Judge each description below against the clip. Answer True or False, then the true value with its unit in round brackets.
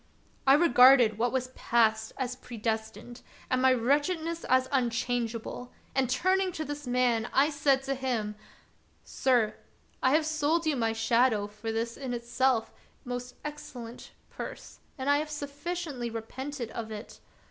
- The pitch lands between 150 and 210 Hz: False (255 Hz)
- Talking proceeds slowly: False (145 wpm)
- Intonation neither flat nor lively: True (3.6 semitones)